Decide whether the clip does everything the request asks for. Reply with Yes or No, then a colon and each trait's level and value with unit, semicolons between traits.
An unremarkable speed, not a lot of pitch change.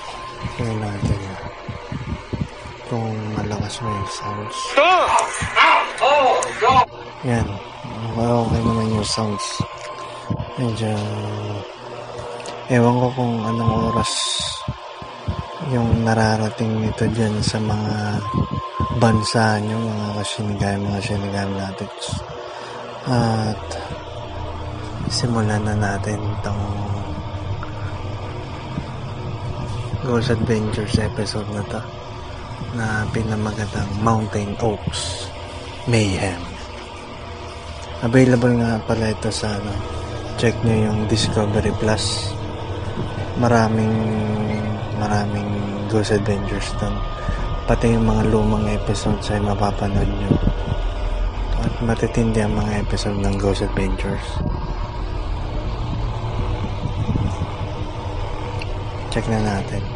No: slow, 85 wpm; narrow, 2.3 semitones